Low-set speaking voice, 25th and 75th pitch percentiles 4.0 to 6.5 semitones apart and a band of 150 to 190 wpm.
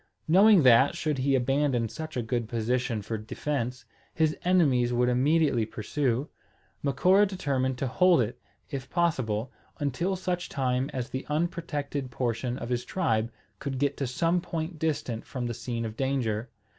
Yes: low, 130 Hz; average, 4.4 semitones; average, 155 wpm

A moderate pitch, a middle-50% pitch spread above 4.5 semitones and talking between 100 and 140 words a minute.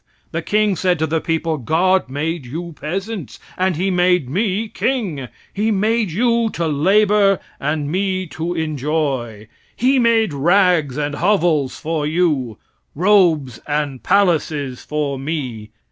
Yes: medium, 165 Hz; average, 4.9 semitones; slow, 135 wpm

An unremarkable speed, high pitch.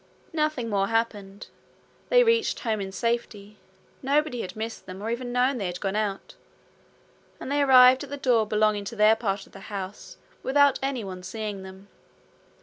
Yes: average, 170 wpm; high, 220 Hz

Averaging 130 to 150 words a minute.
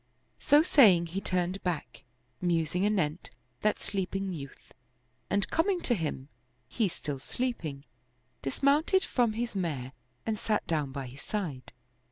Yes: average, 140 wpm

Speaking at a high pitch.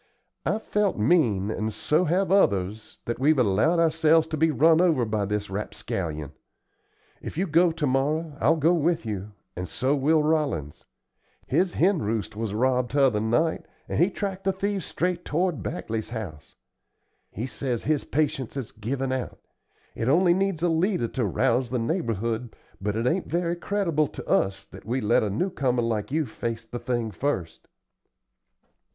No: low, 135 Hz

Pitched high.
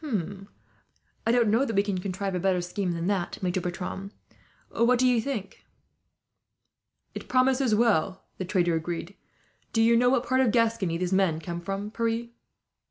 Yes: high, 200 Hz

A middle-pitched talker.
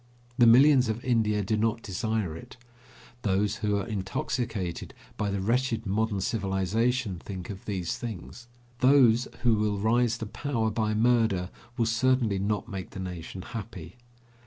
No: low, 110 Hz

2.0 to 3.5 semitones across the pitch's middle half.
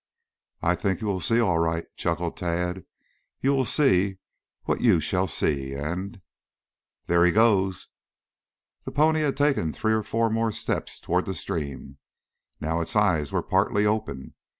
No: average, 5.1 semitones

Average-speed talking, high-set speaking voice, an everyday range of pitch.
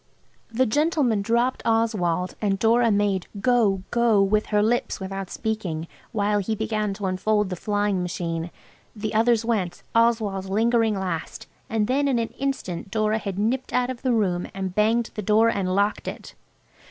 Yes: average, 165 wpm; high, 215 Hz; average, 3.0 semitones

